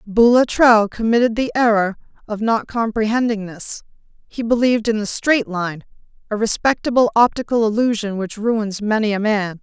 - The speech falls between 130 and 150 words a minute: Yes, average, 145 wpm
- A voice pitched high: Yes, high, 220 Hz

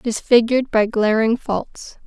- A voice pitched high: Yes, high, 225 Hz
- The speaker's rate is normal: No, slow, 115 wpm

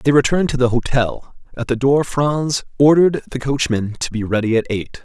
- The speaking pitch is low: Yes, low, 130 Hz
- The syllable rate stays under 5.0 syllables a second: No, 5.5 syllables/s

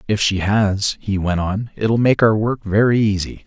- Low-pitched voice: Yes, low, 105 Hz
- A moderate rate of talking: No, fast, 210 wpm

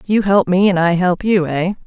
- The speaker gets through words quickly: Yes, fast, 260 wpm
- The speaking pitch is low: No, medium, 185 Hz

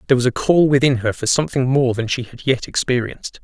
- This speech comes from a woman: No, male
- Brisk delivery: Yes, fast, 245 wpm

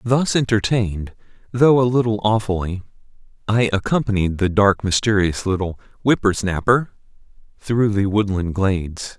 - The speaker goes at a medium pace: No, slow, 120 wpm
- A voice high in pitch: No, low, 105 Hz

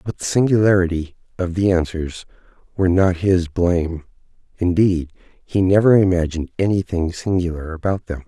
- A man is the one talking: Yes, male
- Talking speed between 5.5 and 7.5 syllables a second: No, 5.2 syllables/s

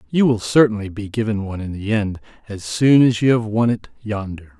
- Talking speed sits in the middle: No, fast, 220 wpm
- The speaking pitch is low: Yes, low, 110 Hz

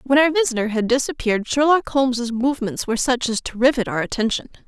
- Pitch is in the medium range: No, very high, 250 Hz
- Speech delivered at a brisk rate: No, average, 195 wpm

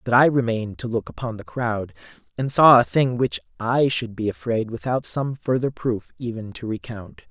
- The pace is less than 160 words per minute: No, average, 195 wpm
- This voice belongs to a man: Yes, male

